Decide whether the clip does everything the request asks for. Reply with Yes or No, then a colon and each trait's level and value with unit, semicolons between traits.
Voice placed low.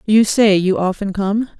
No: high, 205 Hz